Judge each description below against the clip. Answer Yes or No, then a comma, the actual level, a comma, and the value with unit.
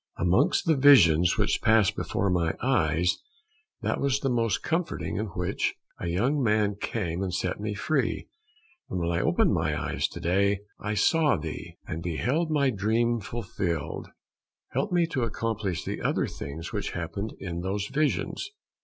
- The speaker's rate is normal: Yes, average, 160 wpm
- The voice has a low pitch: Yes, low, 105 Hz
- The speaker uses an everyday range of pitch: No, wide, 6.5 semitones